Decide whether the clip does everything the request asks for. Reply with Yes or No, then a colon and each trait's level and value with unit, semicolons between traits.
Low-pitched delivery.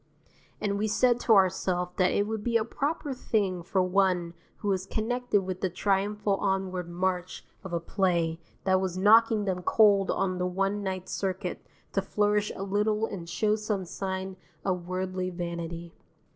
No: high, 190 Hz